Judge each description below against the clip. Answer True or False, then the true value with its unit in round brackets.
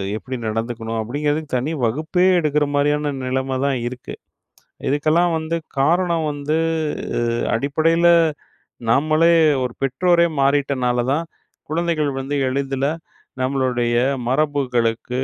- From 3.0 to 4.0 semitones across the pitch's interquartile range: True (3.5 semitones)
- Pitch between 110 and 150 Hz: True (140 Hz)